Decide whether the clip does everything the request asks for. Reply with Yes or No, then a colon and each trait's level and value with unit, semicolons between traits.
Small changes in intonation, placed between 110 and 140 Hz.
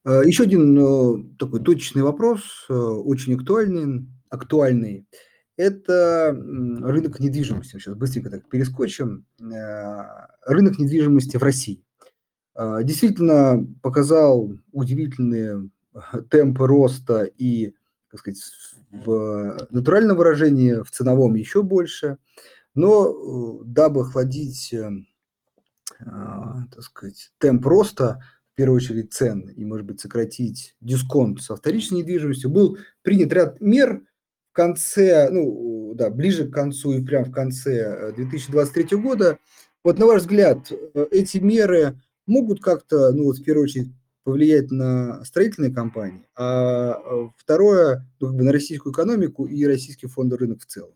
No: average, 4.4 semitones; low, 135 Hz